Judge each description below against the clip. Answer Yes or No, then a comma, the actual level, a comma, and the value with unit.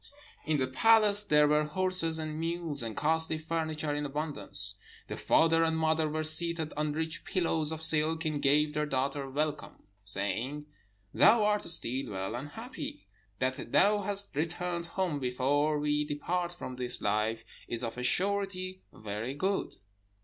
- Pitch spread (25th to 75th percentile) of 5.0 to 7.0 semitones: No, average, 3.4 semitones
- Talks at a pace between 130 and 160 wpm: Yes, average, 155 wpm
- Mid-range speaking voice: Yes, medium, 155 Hz